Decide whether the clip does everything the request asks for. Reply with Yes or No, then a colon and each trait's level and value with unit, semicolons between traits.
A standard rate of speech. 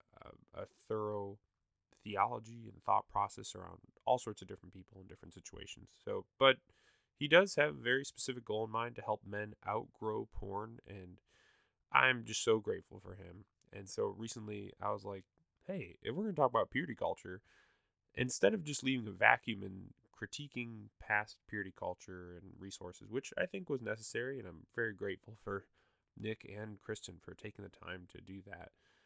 Yes: average, 180 wpm